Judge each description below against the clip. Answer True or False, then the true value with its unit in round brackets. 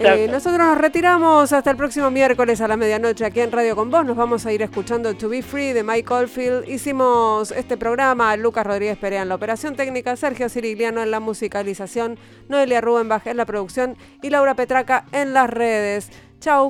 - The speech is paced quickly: True (200 wpm)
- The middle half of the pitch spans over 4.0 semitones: False (3.4 semitones)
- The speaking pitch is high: True (235 Hz)